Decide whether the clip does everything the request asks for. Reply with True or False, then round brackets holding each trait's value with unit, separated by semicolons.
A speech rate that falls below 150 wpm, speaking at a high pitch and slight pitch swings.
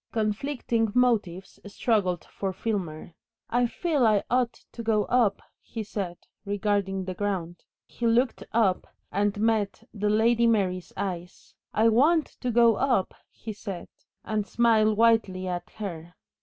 False (140 wpm; 215 Hz; 3.2 semitones)